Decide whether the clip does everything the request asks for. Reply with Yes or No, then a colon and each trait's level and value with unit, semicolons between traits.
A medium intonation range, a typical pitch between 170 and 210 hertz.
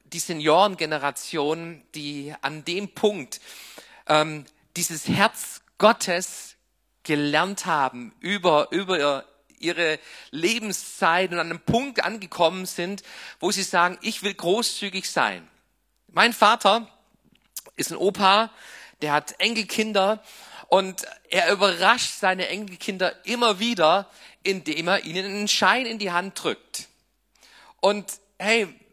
Yes: average, 3.7 semitones; medium, 185 Hz